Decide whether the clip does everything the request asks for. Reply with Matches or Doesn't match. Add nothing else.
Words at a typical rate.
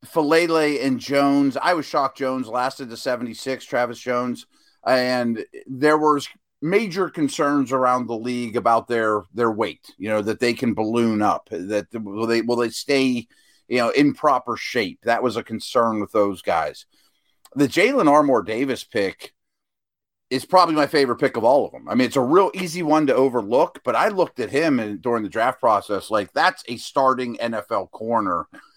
Matches